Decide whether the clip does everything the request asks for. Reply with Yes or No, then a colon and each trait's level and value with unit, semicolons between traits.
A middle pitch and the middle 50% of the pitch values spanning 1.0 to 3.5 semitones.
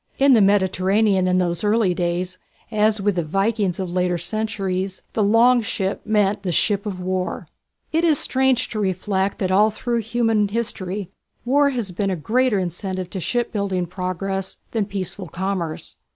No: high, 195 Hz; average, 3.0 semitones